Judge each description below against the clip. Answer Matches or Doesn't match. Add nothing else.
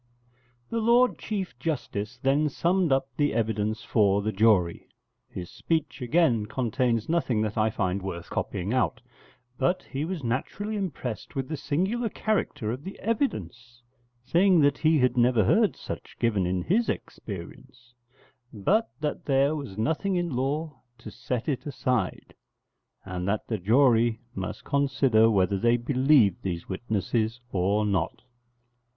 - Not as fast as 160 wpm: Matches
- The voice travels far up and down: Matches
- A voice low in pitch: Matches